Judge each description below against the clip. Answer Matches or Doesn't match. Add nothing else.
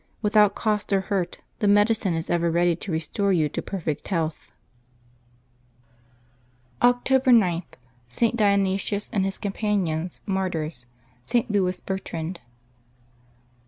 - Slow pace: Matches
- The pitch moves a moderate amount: Matches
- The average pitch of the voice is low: Doesn't match